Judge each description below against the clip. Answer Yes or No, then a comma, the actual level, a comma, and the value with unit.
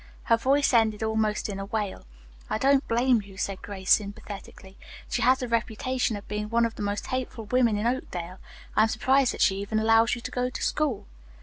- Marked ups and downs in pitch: No, average, 3.5 semitones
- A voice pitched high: Yes, high, 220 Hz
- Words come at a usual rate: No, fast, 210 wpm